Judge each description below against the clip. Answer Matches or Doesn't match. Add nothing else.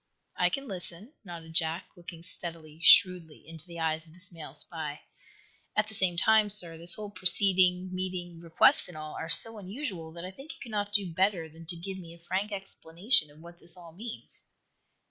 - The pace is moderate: Matches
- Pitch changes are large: Doesn't match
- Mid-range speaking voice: Matches